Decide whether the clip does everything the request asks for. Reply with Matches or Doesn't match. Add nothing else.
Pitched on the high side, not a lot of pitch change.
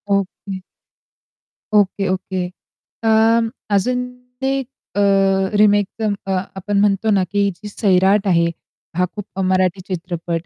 Matches